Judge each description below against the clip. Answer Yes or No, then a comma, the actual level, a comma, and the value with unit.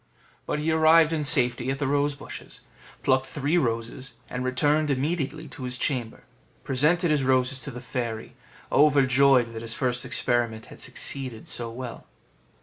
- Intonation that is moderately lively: Yes, average, 3.2 semitones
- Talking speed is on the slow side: No, average, 155 wpm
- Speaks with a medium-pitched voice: No, low, 130 Hz